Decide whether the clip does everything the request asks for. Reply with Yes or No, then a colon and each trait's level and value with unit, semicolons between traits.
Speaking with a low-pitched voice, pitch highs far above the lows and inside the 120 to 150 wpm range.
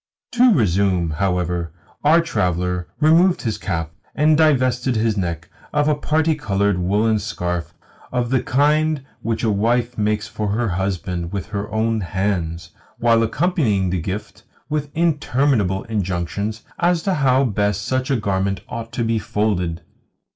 Yes: low, 110 Hz; wide, 6.0 semitones; average, 145 wpm